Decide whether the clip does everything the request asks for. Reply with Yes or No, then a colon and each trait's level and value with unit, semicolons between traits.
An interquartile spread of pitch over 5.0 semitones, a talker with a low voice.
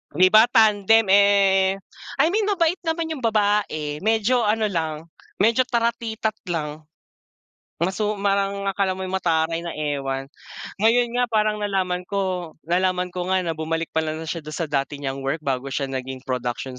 No: wide, 5.5 semitones; medium, 185 Hz